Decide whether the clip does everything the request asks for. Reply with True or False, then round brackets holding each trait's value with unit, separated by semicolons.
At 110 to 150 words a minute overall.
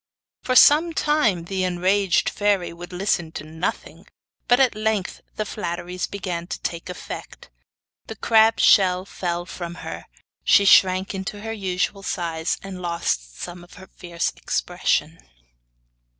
True (140 wpm)